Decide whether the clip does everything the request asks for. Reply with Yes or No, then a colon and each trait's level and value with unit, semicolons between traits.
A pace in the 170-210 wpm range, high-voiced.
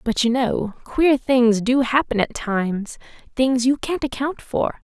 No: average, 160 wpm; very high, 250 Hz